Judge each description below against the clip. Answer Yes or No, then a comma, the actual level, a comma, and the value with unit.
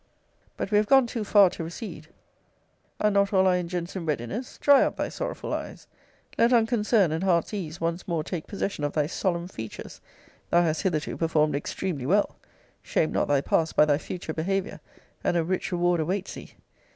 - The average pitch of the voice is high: No, medium, 175 Hz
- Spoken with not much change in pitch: No, average, 4.0 semitones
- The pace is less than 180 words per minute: No, average, 190 wpm